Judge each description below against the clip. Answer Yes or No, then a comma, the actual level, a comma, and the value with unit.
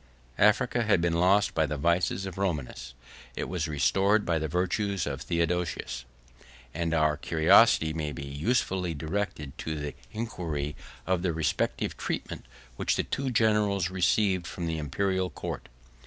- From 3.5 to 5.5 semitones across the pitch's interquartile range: Yes, average, 4.1 semitones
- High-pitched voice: No, very low, 85 Hz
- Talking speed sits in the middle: Yes, average, 155 wpm